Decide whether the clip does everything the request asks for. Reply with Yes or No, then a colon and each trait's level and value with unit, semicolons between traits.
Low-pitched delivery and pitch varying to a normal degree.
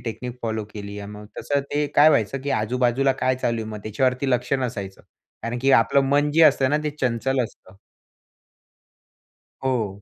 Yes: low, 125 Hz; average, 3.9 semitones